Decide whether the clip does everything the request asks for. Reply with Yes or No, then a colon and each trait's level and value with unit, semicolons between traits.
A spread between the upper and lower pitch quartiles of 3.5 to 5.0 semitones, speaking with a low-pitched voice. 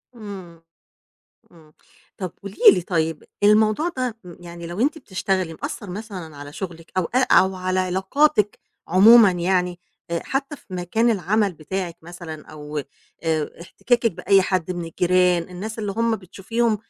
No: average, 3.9 semitones; medium, 185 Hz